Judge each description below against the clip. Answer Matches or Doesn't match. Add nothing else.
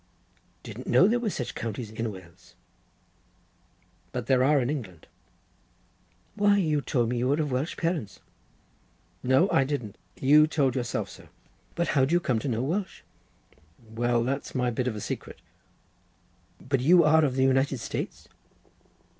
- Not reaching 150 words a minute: Doesn't match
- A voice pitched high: Doesn't match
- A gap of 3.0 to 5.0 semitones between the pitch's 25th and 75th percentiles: Matches